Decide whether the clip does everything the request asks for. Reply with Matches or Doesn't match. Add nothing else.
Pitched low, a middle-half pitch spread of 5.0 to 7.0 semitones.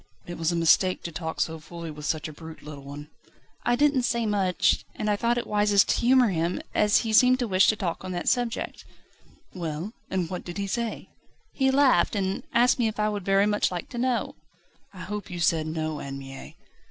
Doesn't match